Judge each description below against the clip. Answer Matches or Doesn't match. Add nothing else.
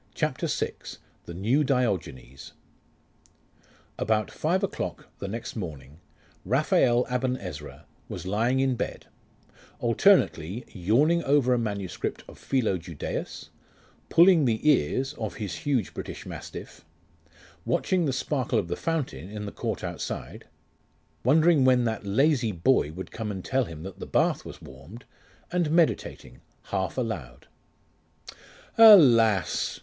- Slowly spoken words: Matches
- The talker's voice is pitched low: Matches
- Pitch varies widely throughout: Matches